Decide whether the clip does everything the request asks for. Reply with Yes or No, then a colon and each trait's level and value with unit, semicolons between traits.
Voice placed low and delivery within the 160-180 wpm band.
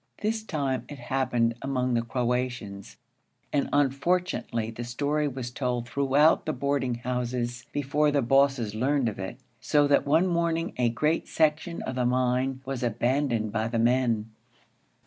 No: low, 130 Hz; average, 150 wpm